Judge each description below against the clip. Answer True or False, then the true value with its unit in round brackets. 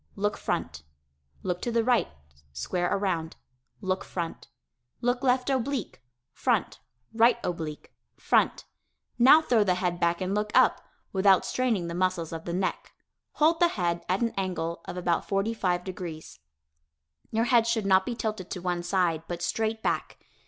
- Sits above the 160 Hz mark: True (190 Hz)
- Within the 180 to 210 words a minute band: False (160 wpm)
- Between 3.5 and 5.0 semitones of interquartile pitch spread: True (4.6 semitones)